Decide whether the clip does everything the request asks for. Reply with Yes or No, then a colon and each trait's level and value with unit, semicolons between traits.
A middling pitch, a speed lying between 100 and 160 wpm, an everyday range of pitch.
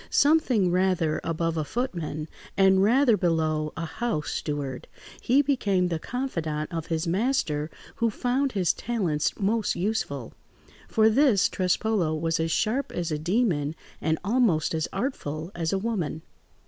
No: medium, 180 Hz; average, 145 wpm; wide, 6.3 semitones